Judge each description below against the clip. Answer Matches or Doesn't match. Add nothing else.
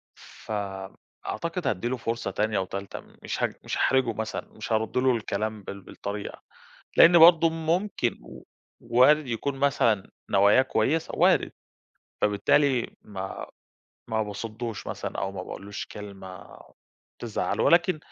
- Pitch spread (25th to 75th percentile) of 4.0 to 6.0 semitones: Matches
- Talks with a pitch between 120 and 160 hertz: Doesn't match